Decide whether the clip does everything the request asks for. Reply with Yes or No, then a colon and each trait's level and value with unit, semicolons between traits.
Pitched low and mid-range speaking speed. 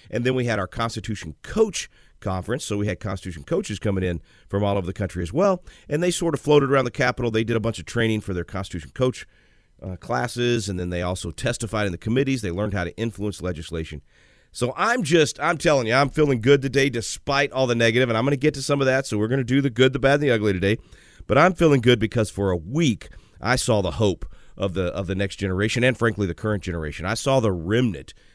No: low, 110 Hz; fast, 250 wpm